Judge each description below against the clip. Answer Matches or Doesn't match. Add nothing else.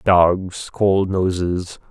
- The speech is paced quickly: Doesn't match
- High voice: Doesn't match